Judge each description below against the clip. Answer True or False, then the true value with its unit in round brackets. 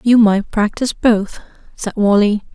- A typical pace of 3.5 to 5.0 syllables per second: True (4.5 syllables/s)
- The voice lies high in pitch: True (215 Hz)